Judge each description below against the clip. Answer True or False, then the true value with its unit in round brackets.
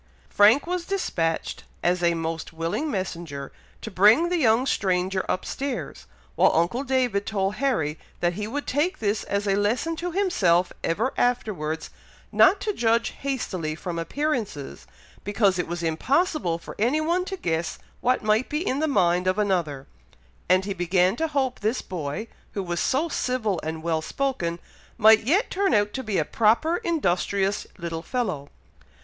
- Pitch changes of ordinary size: False (7.6 semitones)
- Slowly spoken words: False (165 wpm)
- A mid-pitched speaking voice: False (205 Hz)